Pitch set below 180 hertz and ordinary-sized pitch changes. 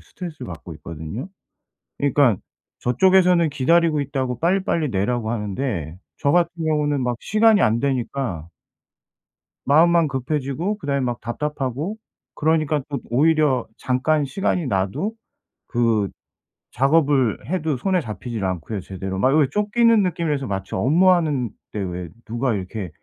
No: medium, 140 Hz; wide, 6.1 semitones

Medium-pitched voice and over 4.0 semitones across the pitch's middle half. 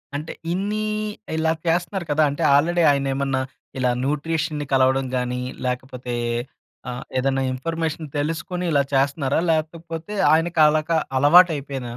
No: medium, 150 Hz; average, 3.5 semitones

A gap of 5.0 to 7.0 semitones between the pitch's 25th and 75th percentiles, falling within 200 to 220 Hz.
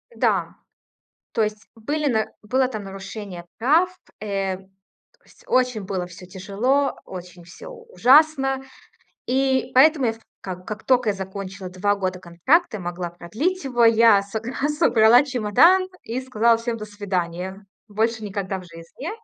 Yes: wide, 5.4 semitones; high, 215 Hz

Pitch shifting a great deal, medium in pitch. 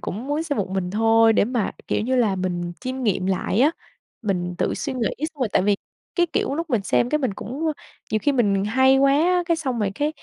No: wide, 6.0 semitones; high, 240 Hz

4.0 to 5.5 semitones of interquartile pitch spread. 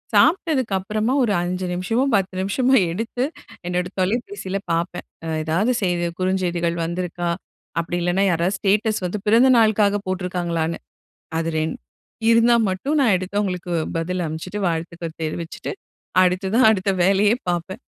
No: average, 3.6 semitones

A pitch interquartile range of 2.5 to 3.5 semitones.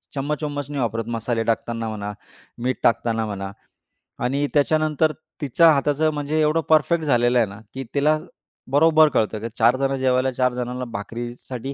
No: average, 4.2 semitones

